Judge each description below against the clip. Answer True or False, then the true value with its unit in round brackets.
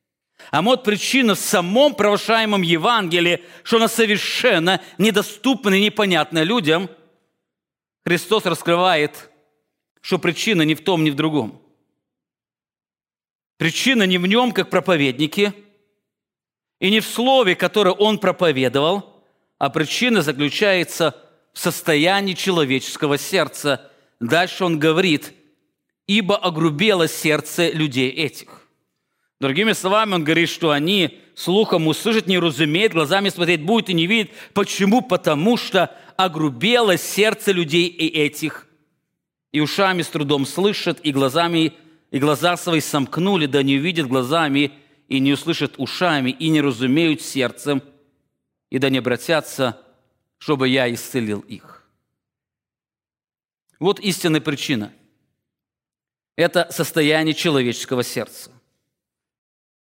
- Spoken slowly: True (115 wpm)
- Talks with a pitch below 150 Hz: False (165 Hz)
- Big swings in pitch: False (4.9 semitones)